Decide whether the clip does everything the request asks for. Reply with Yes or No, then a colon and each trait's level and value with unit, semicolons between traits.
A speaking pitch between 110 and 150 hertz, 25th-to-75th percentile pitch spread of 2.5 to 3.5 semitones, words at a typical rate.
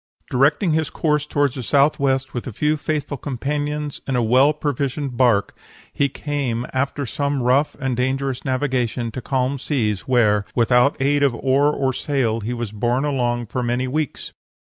Yes: low, 135 Hz; average, 2.9 semitones; average, 165 wpm